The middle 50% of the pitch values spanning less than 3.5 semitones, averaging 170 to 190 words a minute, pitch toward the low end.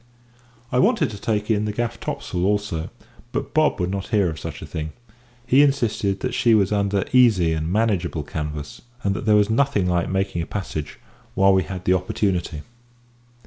No: average, 4.1 semitones; average, 185 wpm; low, 100 Hz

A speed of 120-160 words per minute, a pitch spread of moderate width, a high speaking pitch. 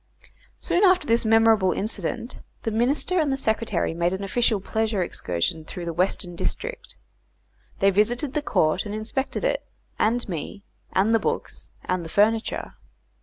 Yes: average, 150 wpm; average, 4.4 semitones; high, 215 Hz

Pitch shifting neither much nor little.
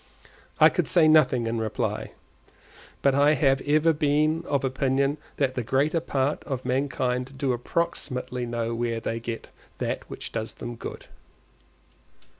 Yes: average, 3.4 semitones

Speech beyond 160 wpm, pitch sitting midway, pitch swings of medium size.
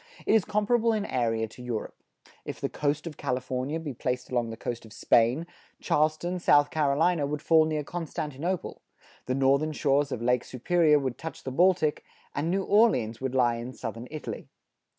Yes: average, 175 wpm; medium, 145 Hz; average, 4.5 semitones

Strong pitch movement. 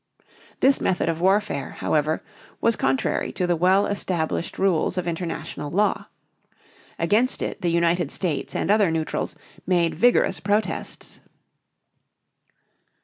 No: average, 3.7 semitones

